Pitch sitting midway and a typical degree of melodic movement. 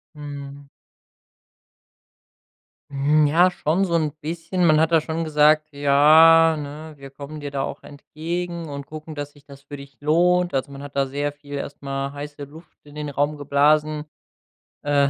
No: medium, 150 Hz; narrow, 2.0 semitones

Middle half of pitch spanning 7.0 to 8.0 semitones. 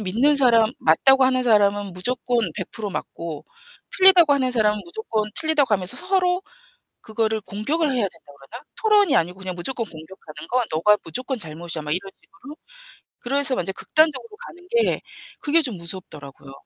Yes: wide, 7.5 semitones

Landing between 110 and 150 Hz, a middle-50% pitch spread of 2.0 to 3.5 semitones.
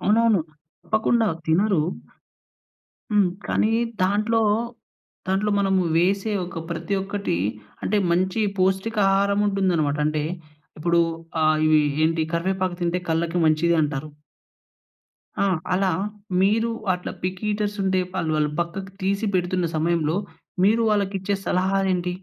No: high, 190 Hz; average, 3.0 semitones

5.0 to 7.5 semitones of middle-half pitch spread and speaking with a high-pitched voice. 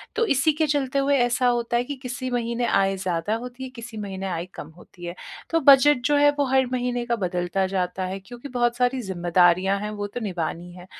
Yes: average, 5.3 semitones; high, 235 Hz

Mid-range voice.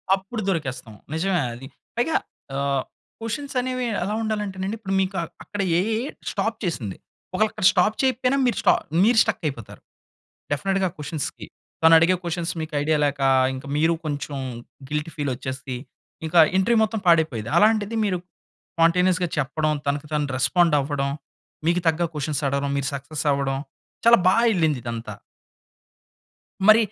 Yes: medium, 165 Hz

